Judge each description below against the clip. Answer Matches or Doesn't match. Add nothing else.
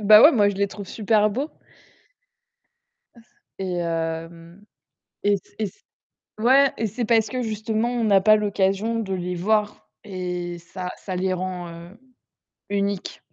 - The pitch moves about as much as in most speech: Matches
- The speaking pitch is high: Matches